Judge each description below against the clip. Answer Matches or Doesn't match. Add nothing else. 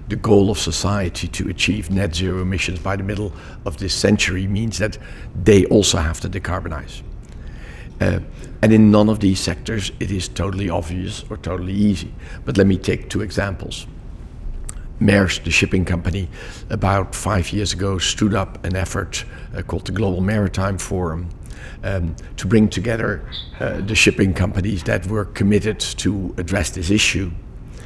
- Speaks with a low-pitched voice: Matches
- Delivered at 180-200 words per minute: Doesn't match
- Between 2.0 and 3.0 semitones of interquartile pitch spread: Matches